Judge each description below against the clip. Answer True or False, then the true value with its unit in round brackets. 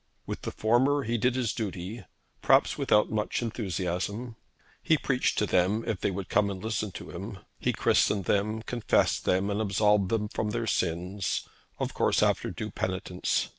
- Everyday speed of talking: True (170 wpm)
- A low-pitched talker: True (105 Hz)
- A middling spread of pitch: True (3.1 semitones)